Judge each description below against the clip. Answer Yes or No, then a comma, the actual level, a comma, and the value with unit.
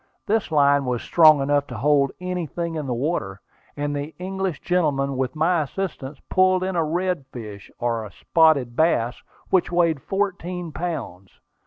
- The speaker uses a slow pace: No, average, 150 wpm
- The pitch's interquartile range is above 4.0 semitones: Yes, average, 5.0 semitones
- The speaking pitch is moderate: Yes, medium, 155 Hz